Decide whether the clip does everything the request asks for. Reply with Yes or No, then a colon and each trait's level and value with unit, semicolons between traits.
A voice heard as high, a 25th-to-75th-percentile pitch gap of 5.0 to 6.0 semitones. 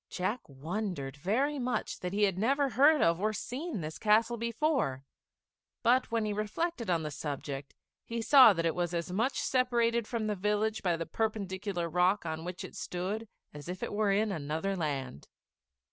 Yes: high, 205 Hz; wide, 5.4 semitones